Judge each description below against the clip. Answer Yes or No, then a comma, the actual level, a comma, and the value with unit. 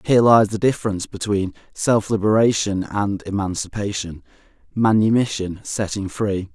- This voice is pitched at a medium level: No, low, 105 Hz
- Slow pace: Yes, slow, 110 wpm